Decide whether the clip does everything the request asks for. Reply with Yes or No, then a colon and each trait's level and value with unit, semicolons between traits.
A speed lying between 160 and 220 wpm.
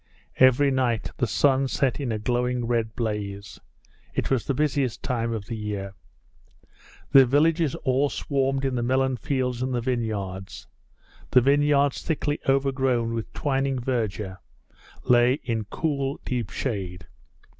No: average, 140 wpm